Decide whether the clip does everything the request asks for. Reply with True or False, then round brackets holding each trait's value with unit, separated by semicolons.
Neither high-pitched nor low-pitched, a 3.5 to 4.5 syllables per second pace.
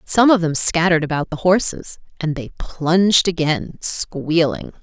True (170 Hz; 4.4 syllables/s)